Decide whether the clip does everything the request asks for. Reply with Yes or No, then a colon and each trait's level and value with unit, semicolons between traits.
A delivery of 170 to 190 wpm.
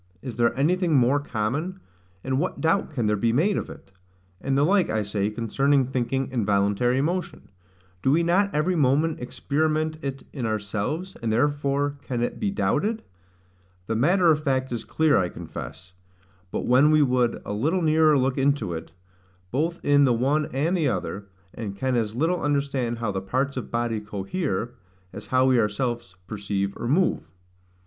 Yes: average, 175 wpm